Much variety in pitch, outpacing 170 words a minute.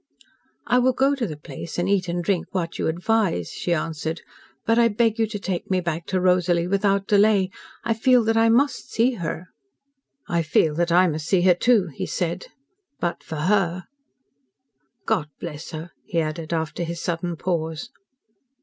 No: average, 4.2 semitones; average, 180 wpm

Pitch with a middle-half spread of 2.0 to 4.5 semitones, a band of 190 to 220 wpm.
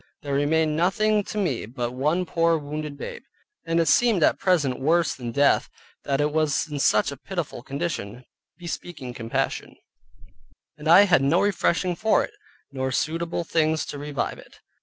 No: average, 3.7 semitones; average, 165 wpm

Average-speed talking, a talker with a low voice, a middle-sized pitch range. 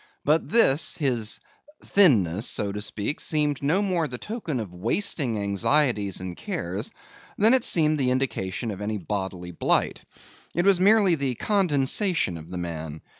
No: average, 155 wpm; low, 130 Hz; wide, 8.8 semitones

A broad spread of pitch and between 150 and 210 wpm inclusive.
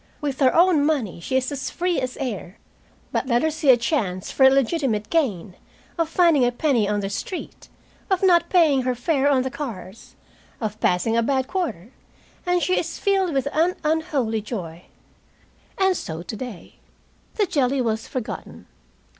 Yes: wide, 6.2 semitones; average, 170 wpm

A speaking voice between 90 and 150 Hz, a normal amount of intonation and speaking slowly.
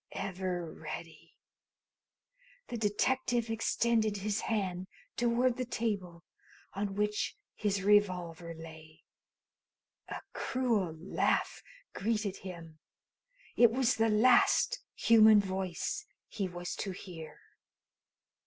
No: high, 200 Hz; average, 4.2 semitones; slow, 95 wpm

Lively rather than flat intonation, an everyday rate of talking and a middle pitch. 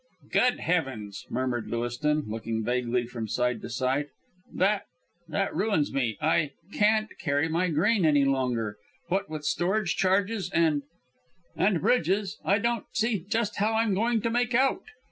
Yes: wide, 8.5 semitones; average, 150 wpm; medium, 165 Hz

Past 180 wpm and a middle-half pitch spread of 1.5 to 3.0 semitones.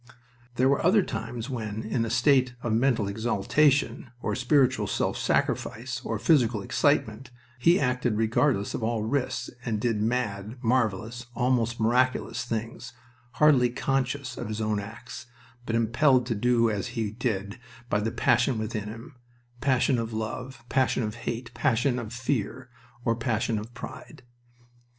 No: average, 150 wpm; average, 2.7 semitones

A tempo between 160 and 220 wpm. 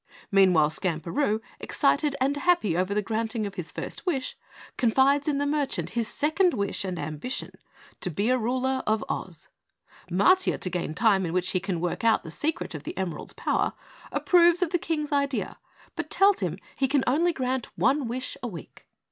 Yes: average, 180 wpm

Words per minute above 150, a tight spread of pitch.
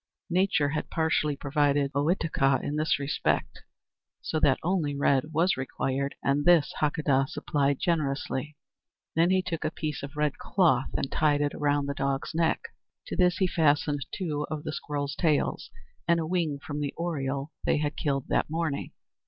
Yes: average, 170 wpm; narrow, 2.3 semitones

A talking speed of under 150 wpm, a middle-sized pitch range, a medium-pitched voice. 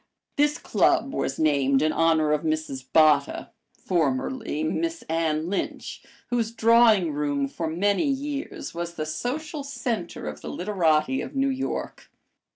No: average, 140 wpm; wide, 8.3 semitones; medium, 170 Hz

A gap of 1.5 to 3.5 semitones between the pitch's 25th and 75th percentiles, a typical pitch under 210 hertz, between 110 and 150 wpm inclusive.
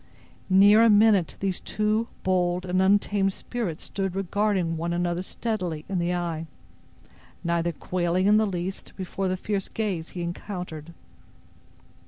Yes: average, 2.8 semitones; medium, 185 Hz; average, 140 wpm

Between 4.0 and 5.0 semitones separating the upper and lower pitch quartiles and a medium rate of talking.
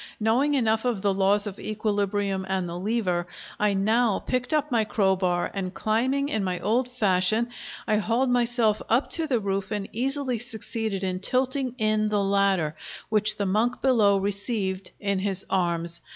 No: average, 3.6 semitones; average, 165 wpm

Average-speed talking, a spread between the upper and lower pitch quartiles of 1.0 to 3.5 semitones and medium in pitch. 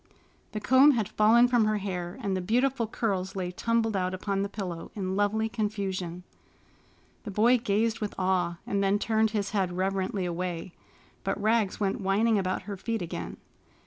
No: average, 175 wpm; average, 2.9 semitones; high, 200 Hz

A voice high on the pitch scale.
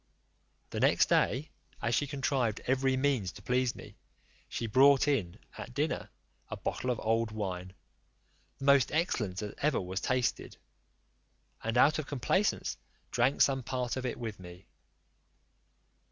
No: low, 125 Hz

